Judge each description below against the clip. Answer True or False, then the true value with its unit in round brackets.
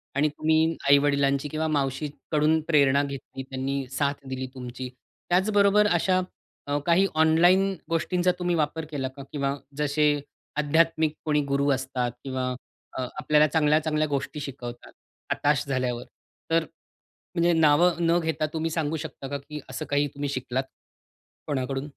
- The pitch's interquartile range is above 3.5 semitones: False (2.7 semitones)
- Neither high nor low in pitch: True (150 Hz)